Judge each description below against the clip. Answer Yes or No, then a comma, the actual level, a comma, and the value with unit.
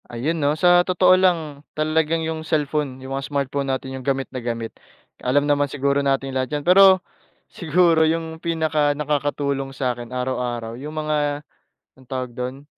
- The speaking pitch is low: No, medium, 145 Hz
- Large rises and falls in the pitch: No, average, 3.2 semitones